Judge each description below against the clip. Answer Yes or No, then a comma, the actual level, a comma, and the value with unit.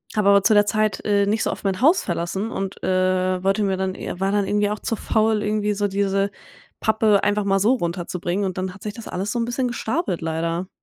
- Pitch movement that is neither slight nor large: No, narrow, 2.3 semitones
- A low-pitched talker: No, high, 200 Hz